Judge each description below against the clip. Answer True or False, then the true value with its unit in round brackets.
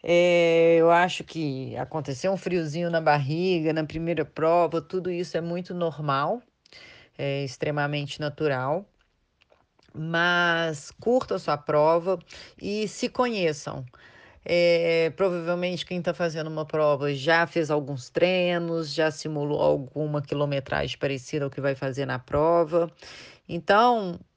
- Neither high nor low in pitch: True (165 Hz)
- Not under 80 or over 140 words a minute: True (125 wpm)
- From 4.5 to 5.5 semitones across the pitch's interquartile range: False (2.8 semitones)